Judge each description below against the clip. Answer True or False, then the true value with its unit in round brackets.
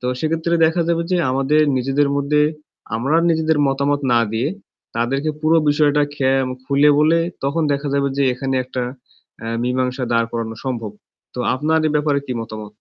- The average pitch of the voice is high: False (140 Hz)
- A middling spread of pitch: True (3.1 semitones)